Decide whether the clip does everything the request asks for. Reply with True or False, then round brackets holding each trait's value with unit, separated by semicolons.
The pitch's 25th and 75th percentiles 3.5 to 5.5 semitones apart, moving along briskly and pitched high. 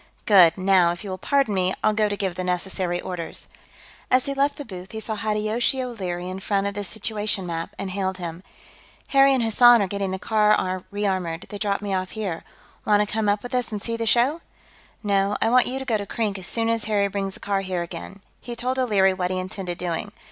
False (3.1 semitones; 235 wpm; 200 Hz)